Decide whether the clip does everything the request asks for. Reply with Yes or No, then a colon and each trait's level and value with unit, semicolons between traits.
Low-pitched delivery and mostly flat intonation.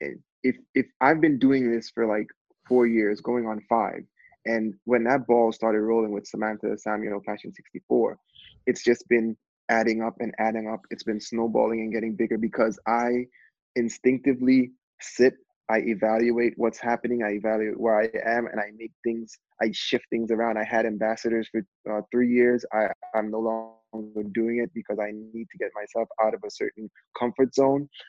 Yes: low, 115 Hz; narrow, 1.6 semitones